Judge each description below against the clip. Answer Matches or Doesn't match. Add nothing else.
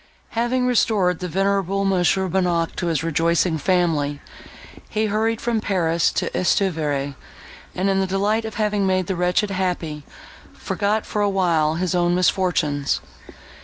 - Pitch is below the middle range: Doesn't match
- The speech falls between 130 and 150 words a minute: Matches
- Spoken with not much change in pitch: Doesn't match